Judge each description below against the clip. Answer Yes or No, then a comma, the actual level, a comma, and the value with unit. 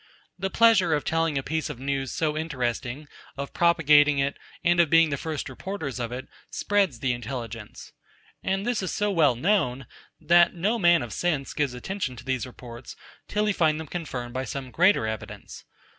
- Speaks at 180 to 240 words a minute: Yes, average, 185 wpm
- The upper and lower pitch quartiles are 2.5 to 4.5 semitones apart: No, average, 5.1 semitones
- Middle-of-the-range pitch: Yes, medium, 150 Hz